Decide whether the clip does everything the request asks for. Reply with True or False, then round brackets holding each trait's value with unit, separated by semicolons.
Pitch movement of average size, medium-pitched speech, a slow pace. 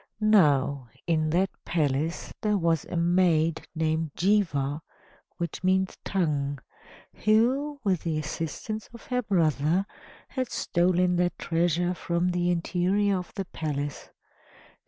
True (3.4 semitones; 175 Hz; 120 wpm)